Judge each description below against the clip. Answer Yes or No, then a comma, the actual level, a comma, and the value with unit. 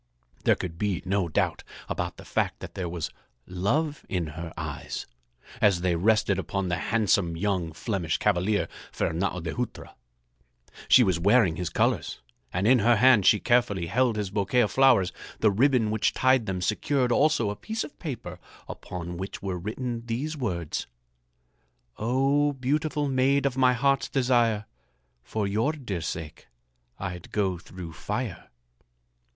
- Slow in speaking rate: No, average, 155 wpm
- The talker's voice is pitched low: Yes, low, 105 Hz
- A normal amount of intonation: No, wide, 5.9 semitones